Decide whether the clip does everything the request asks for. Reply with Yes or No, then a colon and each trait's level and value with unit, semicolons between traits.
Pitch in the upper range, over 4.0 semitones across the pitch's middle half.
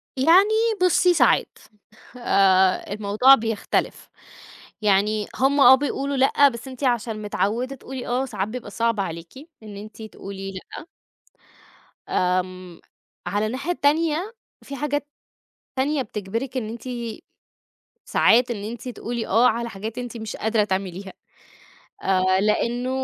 Yes: high, 230 Hz; average, 4.7 semitones